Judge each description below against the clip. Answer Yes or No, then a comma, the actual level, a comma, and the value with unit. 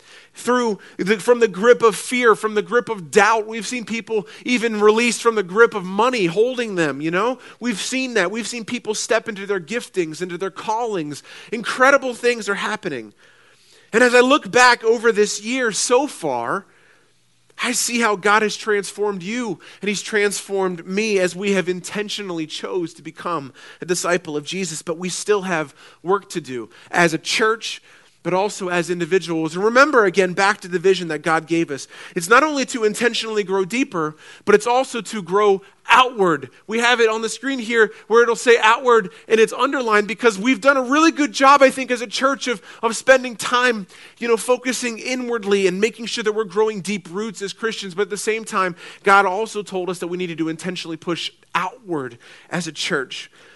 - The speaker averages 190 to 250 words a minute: Yes, average, 195 wpm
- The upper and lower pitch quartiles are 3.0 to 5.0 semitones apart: Yes, average, 4.2 semitones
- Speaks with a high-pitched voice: Yes, high, 215 Hz